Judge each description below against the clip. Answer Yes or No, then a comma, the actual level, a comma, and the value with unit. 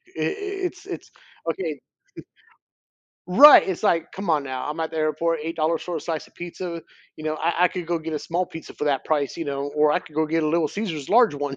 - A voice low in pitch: No, medium, 165 Hz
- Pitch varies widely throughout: No, average, 2.7 semitones